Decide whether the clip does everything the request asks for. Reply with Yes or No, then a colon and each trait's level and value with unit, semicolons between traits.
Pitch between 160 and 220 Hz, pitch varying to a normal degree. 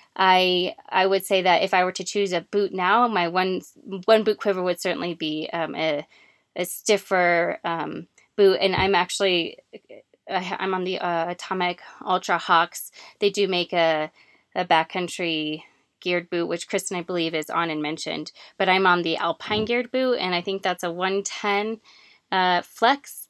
No: medium, 185 Hz; narrow, 2.2 semitones